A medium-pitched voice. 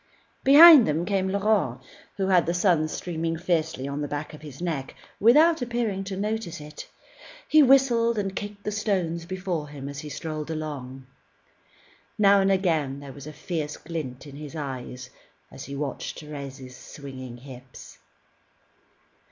Yes: medium, 160 Hz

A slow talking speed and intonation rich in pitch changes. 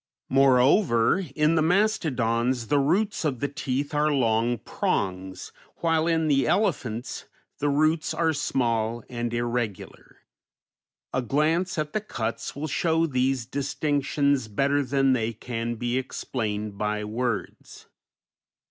No: slow, 125 wpm; average, 4.6 semitones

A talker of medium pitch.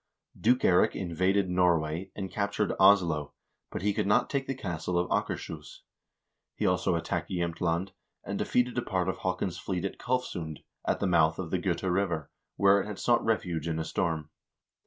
No: very low, 90 Hz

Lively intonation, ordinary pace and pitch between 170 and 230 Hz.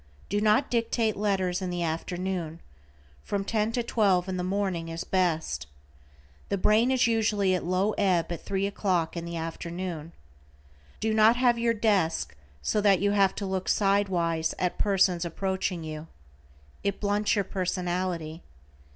No: average, 3.2 semitones; average, 160 wpm; high, 190 Hz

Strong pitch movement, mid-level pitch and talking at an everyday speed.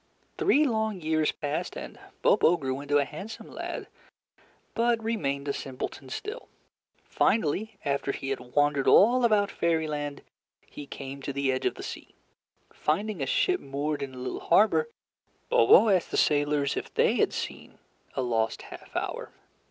Yes: wide, 7.7 semitones; medium, 150 Hz; average, 160 wpm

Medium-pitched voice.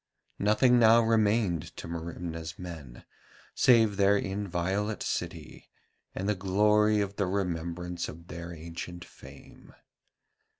No: very low, 95 Hz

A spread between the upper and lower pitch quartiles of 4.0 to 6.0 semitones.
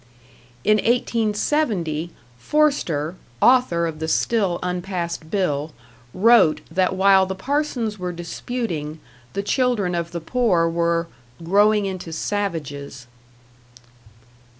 Yes: average, 4.4 semitones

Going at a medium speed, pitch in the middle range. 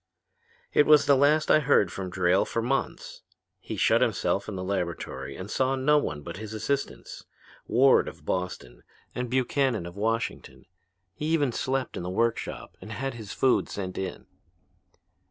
No: average, 165 wpm; low, 115 Hz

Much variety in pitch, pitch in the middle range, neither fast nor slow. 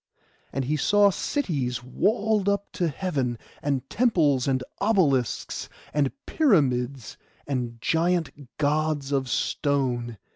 No: wide, 6.1 semitones; medium, 145 Hz; slow, 110 wpm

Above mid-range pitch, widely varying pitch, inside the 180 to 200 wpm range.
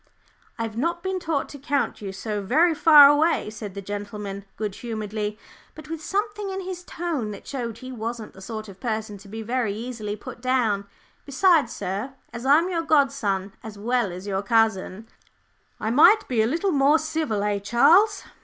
Yes: high, 235 Hz; wide, 6.9 semitones; average, 185 wpm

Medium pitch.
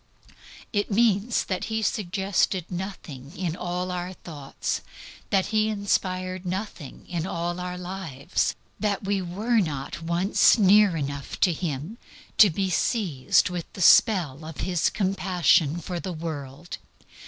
Yes: medium, 180 Hz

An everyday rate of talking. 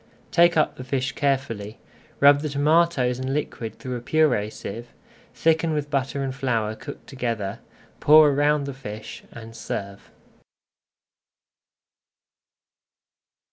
No: slow, 120 wpm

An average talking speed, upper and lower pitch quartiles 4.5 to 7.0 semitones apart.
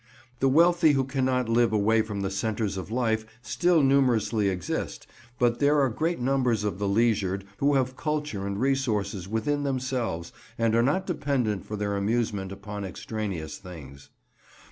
Yes: average, 160 wpm; average, 5.1 semitones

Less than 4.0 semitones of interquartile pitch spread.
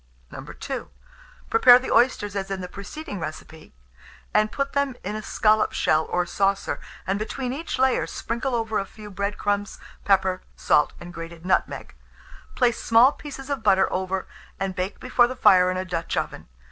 No: average, 4.6 semitones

